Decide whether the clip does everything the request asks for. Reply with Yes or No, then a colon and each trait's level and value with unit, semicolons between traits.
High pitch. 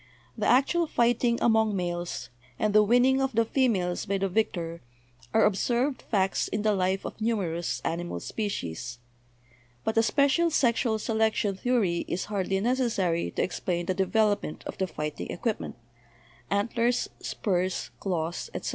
Yes: high, 205 Hz